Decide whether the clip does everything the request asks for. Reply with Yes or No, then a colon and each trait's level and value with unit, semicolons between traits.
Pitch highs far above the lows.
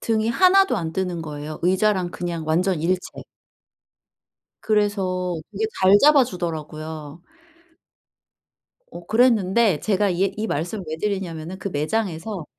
No: average, 4.4 semitones